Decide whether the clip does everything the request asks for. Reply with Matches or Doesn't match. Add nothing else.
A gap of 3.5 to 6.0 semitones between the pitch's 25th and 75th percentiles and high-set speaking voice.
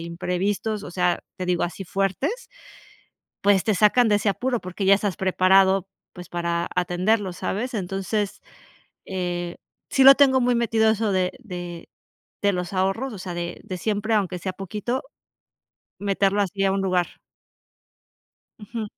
Doesn't match